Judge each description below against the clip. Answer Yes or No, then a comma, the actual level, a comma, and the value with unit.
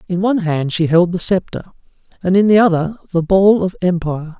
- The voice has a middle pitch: Yes, medium, 180 Hz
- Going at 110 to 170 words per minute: No, fast, 205 wpm